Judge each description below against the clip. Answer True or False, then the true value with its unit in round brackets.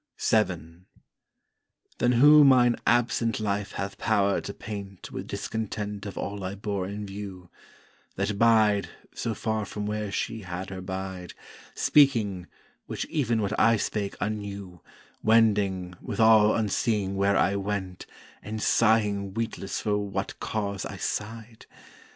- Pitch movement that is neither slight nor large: False (2.1 semitones)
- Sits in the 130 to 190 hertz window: False (105 Hz)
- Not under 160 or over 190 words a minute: False (135 wpm)